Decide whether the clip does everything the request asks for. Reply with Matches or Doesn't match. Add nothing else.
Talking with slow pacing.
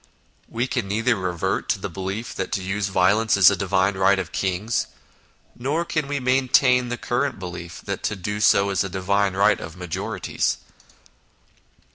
Doesn't match